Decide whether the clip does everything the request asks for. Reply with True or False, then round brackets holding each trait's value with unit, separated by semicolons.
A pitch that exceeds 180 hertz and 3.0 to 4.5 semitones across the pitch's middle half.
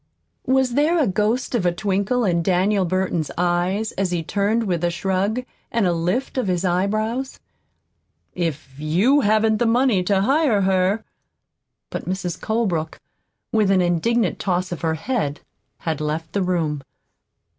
True (190 Hz; 4.2 semitones)